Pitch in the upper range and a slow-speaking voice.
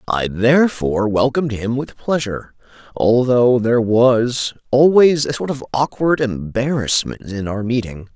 No: low, 120 Hz; slow, 130 wpm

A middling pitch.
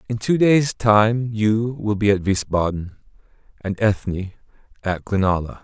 No: low, 105 Hz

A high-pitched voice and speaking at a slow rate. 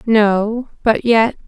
Yes: high, 220 Hz; slow, 120 wpm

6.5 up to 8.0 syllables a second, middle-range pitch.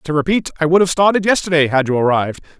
Yes: 6.9 syllables/s; medium, 160 Hz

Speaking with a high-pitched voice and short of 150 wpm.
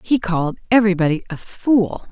Yes: high, 195 Hz; average, 140 wpm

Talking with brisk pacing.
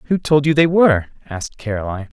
No: average, 190 wpm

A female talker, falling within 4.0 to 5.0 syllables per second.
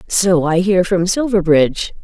Yes: female; 4.4 syllables/s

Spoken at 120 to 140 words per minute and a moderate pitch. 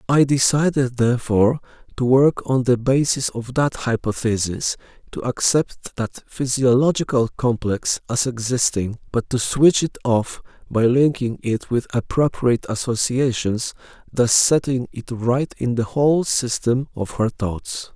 No: slow, 135 wpm; low, 125 Hz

